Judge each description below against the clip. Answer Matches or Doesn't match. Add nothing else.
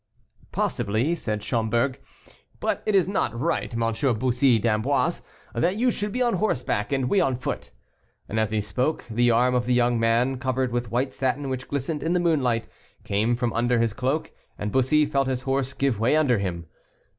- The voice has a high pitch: Doesn't match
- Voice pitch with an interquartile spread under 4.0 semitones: Matches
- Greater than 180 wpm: Matches